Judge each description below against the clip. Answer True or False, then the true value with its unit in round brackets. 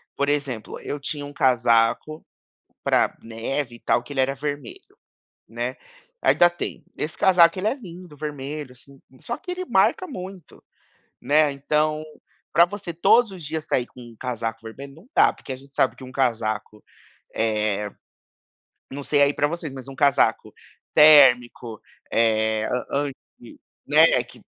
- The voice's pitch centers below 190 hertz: True (140 Hz)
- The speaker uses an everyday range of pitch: True (4.2 semitones)